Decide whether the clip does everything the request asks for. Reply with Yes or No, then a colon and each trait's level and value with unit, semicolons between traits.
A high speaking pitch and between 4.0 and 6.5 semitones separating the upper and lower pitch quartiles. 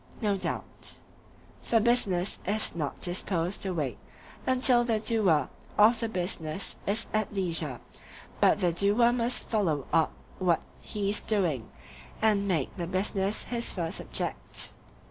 Yes: high, 195 Hz; average, 4.3 semitones